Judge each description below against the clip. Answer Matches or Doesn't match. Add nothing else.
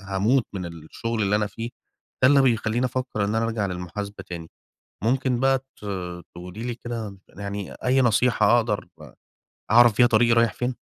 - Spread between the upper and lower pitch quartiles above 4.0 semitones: Doesn't match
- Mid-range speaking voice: Doesn't match